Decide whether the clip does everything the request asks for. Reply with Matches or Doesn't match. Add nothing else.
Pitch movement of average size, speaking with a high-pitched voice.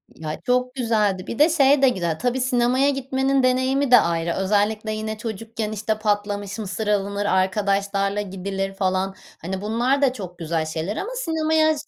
Matches